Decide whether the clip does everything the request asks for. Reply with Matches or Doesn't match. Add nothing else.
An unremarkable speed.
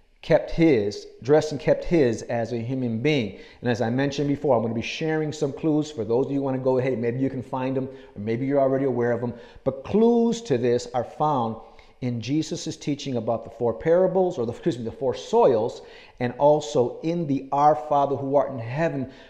Doesn't match